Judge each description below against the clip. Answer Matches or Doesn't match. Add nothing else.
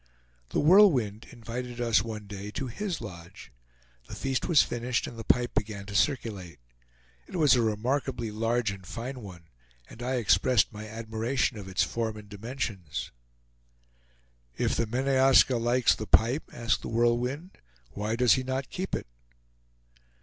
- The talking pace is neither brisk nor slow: Matches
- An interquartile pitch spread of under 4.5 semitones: Matches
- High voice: Doesn't match